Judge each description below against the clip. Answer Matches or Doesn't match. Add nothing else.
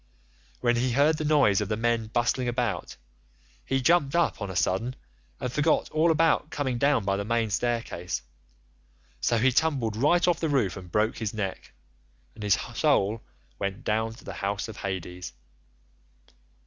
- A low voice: Matches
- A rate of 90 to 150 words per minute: Doesn't match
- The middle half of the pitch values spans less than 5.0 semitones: Doesn't match